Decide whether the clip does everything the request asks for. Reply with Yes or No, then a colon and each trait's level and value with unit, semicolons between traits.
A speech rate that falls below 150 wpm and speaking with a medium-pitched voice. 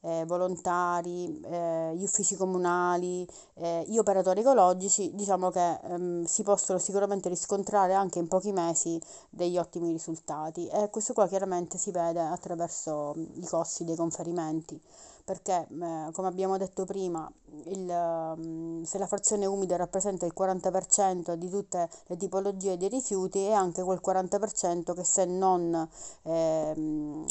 Yes: average, 140 wpm; medium, 180 Hz